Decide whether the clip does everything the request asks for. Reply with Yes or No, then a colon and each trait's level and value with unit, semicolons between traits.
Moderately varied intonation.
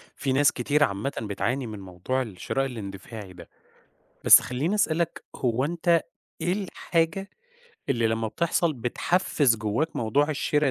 No: wide, 6.3 semitones